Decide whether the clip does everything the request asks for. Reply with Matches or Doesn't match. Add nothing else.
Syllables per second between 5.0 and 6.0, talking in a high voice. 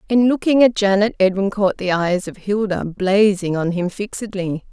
Doesn't match